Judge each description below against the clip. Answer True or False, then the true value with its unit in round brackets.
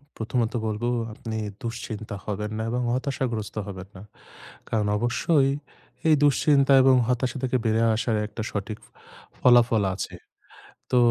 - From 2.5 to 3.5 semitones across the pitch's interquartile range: True (2.9 semitones)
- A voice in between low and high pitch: False (115 Hz)